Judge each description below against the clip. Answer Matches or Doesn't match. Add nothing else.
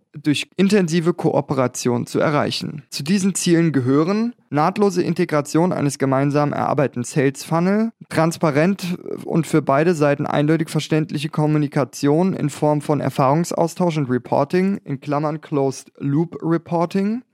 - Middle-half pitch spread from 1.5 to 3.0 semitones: Doesn't match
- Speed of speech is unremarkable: Doesn't match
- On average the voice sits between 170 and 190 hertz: Doesn't match